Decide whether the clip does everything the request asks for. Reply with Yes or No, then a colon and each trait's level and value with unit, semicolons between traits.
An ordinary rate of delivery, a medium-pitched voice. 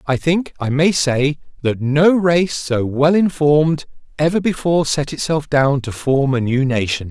Yes: average, 175 wpm; medium, 145 Hz